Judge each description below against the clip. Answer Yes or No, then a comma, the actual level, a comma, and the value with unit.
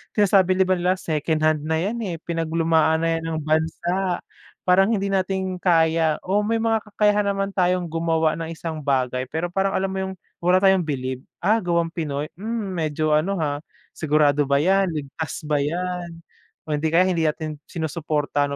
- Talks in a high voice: No, medium, 165 Hz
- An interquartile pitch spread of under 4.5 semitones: Yes, average, 3.4 semitones